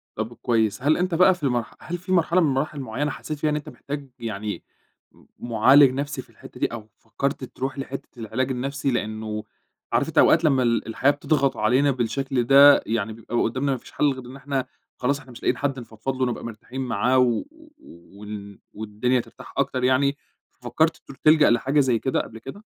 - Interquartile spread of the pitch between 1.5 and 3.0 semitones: No, average, 3.6 semitones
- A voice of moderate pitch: No, low, 130 Hz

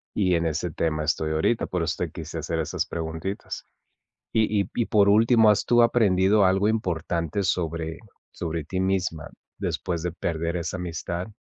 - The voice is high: No, very low, 90 Hz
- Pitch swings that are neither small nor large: Yes, average, 3.7 semitones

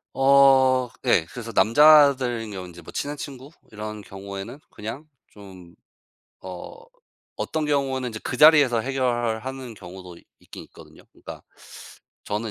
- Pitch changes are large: No, average, 4.5 semitones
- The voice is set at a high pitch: No, low, 120 Hz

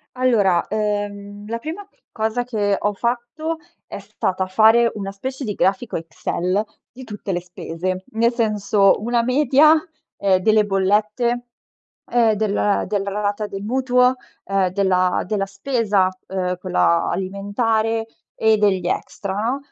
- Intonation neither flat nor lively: Yes, average, 3.3 semitones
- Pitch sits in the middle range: No, high, 210 Hz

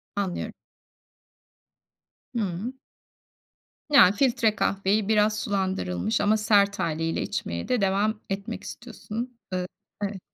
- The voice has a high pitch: Yes, high, 205 Hz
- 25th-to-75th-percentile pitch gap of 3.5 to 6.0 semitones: No, narrow, 2.5 semitones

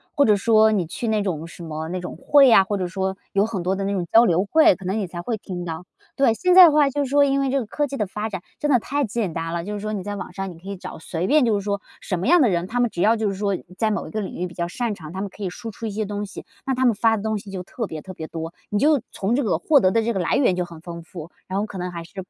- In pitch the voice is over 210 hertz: No, high, 200 Hz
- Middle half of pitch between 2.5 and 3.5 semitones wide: No, average, 4.2 semitones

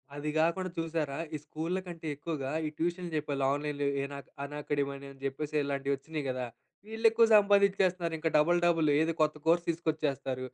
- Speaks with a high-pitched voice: No, medium, 155 Hz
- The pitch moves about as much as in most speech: Yes, average, 3.2 semitones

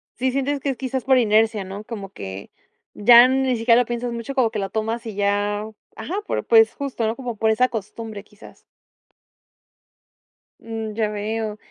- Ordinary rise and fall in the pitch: Yes, average, 3.1 semitones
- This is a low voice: No, high, 225 Hz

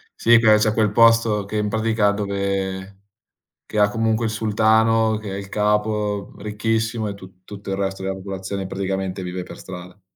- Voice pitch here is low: Yes, low, 105 Hz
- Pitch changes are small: Yes, narrow, 2.1 semitones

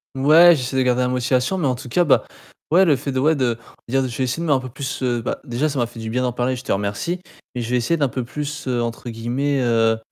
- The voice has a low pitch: Yes, low, 130 Hz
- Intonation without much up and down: No, average, 3.0 semitones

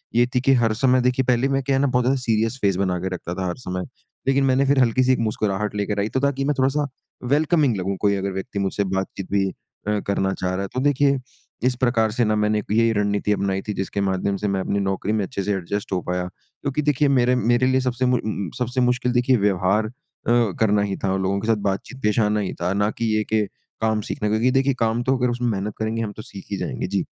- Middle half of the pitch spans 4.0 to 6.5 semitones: Yes, average, 4.3 semitones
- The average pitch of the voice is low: Yes, low, 110 Hz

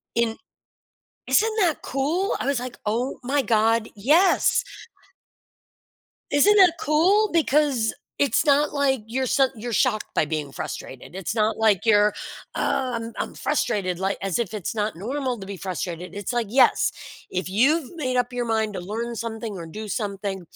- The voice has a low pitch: No, high, 230 Hz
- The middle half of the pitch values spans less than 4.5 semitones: No, average, 5.2 semitones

